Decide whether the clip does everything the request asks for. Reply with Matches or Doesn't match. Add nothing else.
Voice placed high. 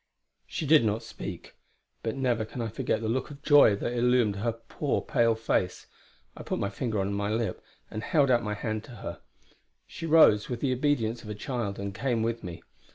Doesn't match